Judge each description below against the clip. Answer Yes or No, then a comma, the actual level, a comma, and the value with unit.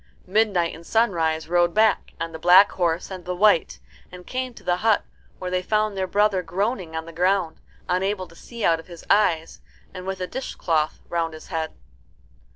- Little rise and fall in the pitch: No, average, 3.3 semitones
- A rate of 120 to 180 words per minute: No, average, 190 wpm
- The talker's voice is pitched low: No, medium, 180 Hz